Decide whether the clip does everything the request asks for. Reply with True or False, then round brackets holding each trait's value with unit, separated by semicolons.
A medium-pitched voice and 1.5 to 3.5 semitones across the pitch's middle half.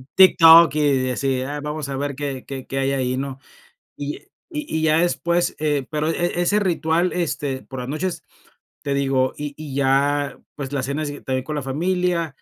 True (145 Hz; 3.0 semitones)